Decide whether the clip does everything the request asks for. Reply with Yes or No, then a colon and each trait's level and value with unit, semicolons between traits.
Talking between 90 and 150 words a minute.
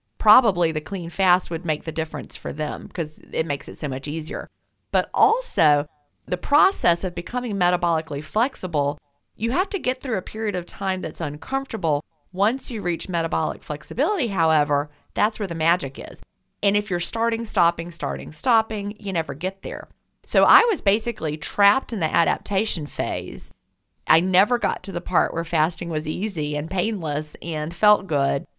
No: average, 170 wpm